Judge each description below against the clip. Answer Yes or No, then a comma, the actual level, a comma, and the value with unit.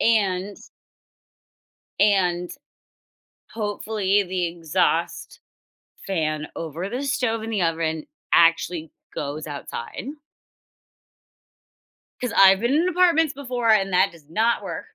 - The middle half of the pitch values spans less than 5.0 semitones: No, wide, 5.5 semitones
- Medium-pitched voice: No, high, 195 Hz